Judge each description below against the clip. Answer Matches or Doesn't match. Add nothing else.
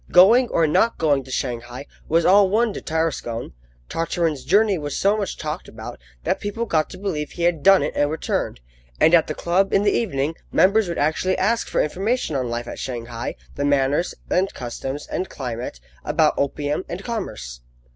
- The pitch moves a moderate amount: Doesn't match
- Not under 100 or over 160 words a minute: Doesn't match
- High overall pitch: Doesn't match